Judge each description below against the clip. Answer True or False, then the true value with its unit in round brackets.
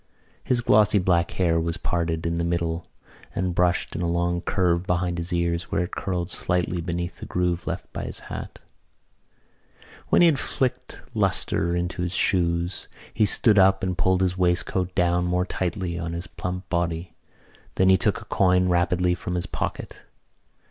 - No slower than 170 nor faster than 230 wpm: True (175 wpm)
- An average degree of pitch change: False (1.2 semitones)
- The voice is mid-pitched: False (90 Hz)